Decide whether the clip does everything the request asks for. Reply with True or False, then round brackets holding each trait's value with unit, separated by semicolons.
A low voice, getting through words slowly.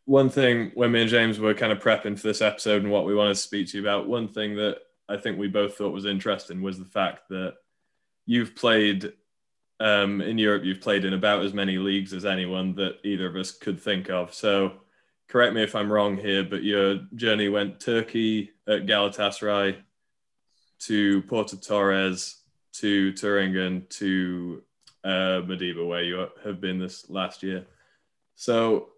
False (100 Hz; 180 wpm)